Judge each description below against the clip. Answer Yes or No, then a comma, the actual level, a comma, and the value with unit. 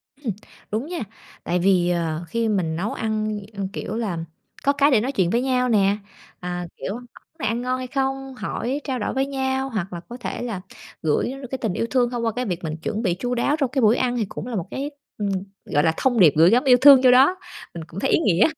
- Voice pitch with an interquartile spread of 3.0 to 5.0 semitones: No, wide, 5.4 semitones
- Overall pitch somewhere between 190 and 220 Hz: No, high, 235 Hz